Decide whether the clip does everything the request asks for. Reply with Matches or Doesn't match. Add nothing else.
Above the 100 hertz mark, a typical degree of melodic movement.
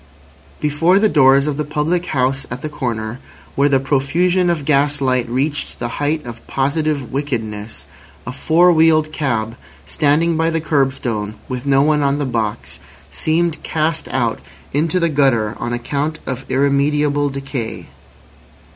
Matches